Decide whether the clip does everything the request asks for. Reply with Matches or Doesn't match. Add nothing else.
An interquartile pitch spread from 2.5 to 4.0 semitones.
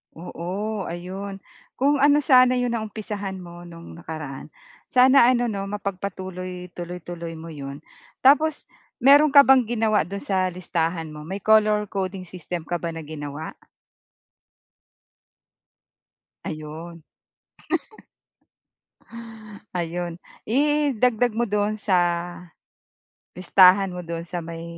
Doesn't match